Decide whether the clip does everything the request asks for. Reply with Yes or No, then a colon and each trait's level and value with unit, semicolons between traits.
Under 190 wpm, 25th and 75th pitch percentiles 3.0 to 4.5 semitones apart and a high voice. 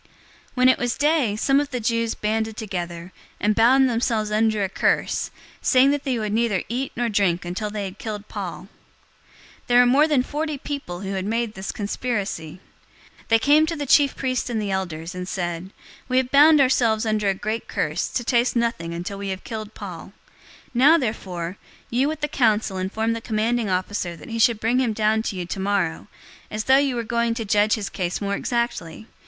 No: fast, 205 wpm; average, 3.9 semitones; high, 220 Hz